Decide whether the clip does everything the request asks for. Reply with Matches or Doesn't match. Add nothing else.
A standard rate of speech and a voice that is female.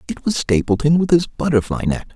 Doesn't match